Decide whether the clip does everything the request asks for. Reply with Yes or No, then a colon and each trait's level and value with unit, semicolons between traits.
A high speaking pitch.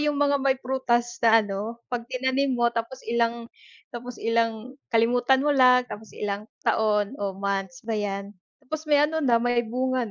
Yes: high, 235 Hz